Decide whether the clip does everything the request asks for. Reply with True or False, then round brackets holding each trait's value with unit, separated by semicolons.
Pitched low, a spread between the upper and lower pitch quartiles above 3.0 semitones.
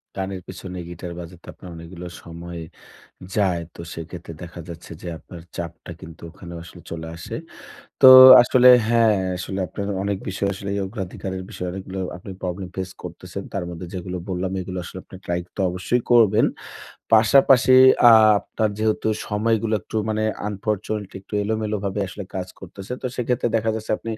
True (95 Hz; 3.4 semitones)